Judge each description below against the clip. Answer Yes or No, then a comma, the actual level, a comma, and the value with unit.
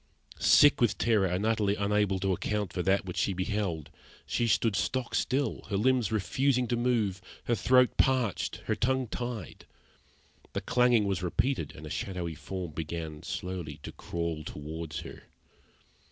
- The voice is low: Yes, low, 100 Hz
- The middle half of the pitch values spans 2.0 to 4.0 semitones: No, average, 5.3 semitones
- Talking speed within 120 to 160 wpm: Yes, average, 155 wpm